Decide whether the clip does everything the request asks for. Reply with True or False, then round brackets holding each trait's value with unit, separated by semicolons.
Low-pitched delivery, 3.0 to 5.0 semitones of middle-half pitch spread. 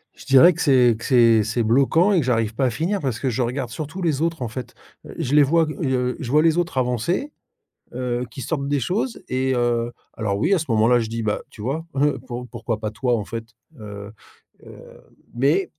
True (125 Hz; 4.6 semitones)